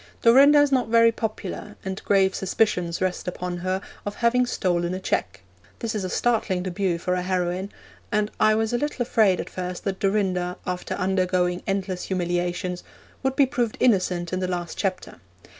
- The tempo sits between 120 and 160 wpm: No, average, 175 wpm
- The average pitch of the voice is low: No, high, 190 Hz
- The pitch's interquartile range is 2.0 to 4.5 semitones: Yes, average, 3.4 semitones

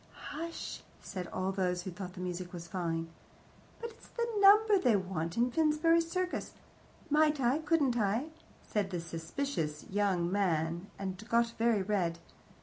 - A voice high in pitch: Yes, high, 200 Hz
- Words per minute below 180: Yes, average, 155 wpm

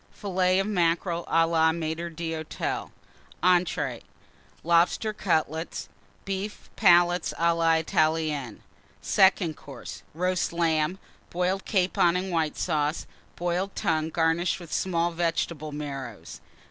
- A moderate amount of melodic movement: No, narrow, 2.1 semitones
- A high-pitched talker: No, medium, 170 Hz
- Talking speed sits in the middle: No, slow, 110 wpm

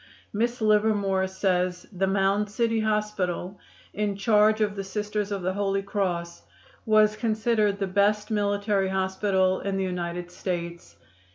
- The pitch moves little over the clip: Yes, narrow, 2.0 semitones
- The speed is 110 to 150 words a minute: Yes, average, 140 wpm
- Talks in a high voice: Yes, high, 200 Hz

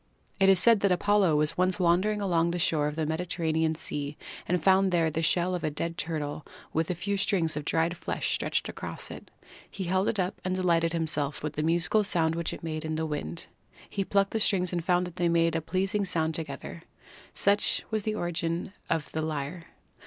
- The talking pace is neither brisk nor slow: No, fast, 210 wpm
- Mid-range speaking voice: Yes, medium, 170 Hz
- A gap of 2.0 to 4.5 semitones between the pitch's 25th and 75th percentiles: Yes, average, 2.8 semitones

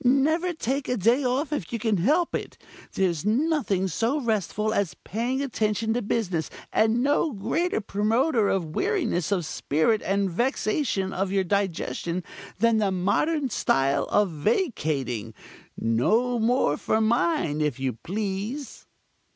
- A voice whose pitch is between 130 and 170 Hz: No, high, 215 Hz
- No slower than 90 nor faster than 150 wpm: Yes, average, 140 wpm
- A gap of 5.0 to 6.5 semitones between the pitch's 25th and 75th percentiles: Yes, wide, 5.6 semitones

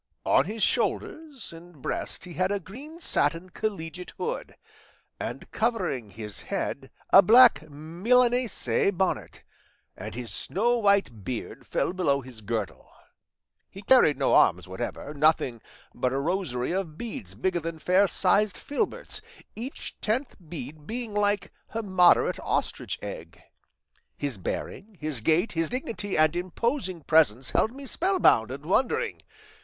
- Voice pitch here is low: No, medium, 180 Hz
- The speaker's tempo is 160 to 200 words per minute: No, average, 140 wpm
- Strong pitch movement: Yes, wide, 7.2 semitones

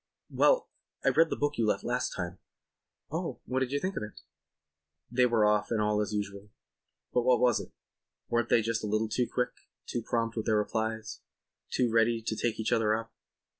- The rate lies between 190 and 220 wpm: Yes, fast, 205 wpm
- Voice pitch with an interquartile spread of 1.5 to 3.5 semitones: Yes, narrow, 2.4 semitones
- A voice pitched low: Yes, low, 115 Hz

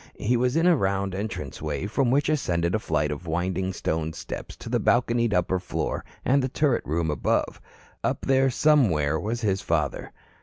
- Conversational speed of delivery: Yes, average, 180 wpm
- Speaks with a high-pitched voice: No, low, 100 Hz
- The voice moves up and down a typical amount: No, wide, 6.9 semitones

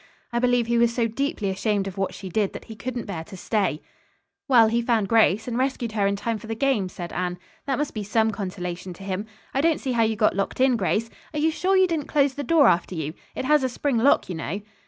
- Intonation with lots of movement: No, average, 4.7 semitones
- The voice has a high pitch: Yes, high, 225 Hz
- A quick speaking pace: Yes, fast, 260 wpm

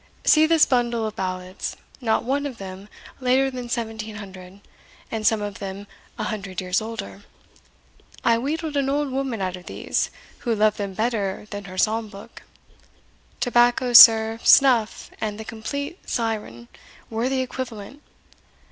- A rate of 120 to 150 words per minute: Yes, average, 145 wpm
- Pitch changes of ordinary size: Yes, average, 3.9 semitones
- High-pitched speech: Yes, high, 225 Hz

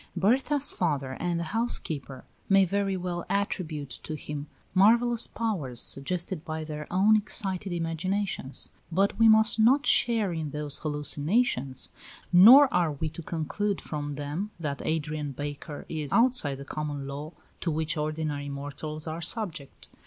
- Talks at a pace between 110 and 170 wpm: Yes, average, 145 wpm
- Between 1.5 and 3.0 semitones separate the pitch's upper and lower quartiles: No, average, 5.3 semitones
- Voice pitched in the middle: Yes, medium, 160 Hz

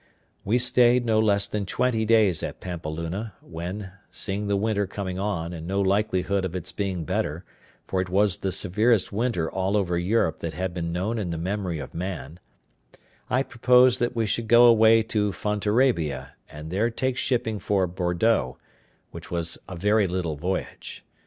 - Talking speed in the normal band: Yes, average, 170 wpm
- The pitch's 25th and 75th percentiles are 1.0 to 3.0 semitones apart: No, average, 4.0 semitones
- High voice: No, low, 100 Hz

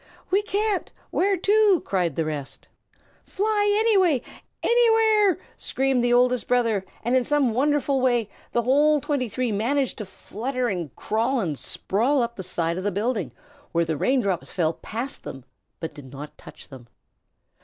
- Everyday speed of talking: Yes, average, 165 wpm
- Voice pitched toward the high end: Yes, very high, 250 Hz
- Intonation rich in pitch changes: Yes, wide, 7.4 semitones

